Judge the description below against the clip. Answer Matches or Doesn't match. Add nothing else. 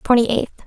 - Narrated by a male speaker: Doesn't match